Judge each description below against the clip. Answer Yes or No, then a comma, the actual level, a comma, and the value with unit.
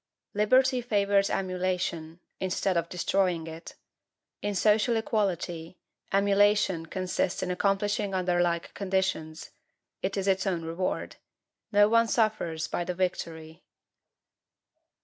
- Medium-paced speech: No, slow, 110 wpm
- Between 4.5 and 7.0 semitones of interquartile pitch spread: No, average, 2.9 semitones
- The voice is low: No, high, 190 Hz